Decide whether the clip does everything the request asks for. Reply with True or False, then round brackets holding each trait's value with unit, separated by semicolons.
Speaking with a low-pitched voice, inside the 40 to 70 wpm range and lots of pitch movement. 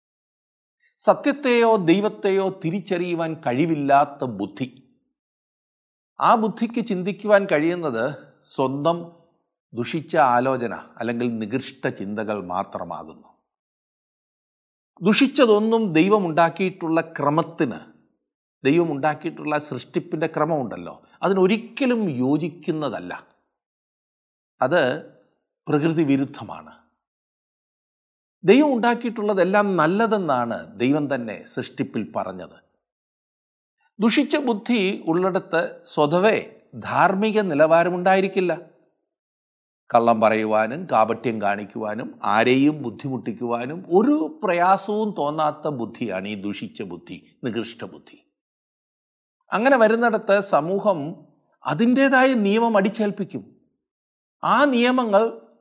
False (170 Hz; 65 wpm; 7.3 semitones)